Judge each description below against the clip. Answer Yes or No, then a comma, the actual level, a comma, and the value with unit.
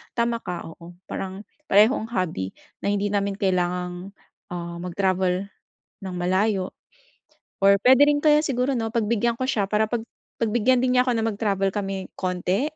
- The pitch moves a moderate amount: Yes, average, 4.1 semitones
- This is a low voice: No, high, 200 Hz